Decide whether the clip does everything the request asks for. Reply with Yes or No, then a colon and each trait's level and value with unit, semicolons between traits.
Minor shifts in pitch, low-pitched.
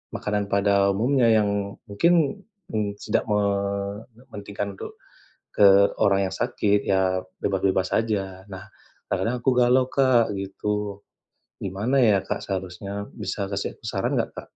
Yes: narrow, 2.2 semitones; low, 100 Hz